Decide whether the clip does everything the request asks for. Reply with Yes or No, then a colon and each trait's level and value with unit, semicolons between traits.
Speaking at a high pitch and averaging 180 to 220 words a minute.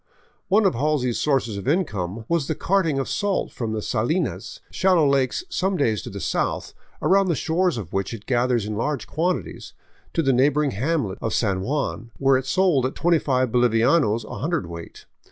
No: low, 135 Hz; average, 190 wpm